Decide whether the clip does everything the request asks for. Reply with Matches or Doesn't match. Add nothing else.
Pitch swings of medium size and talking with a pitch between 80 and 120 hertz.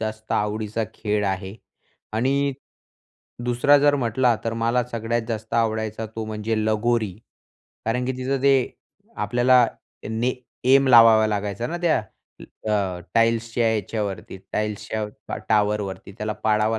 Doesn't match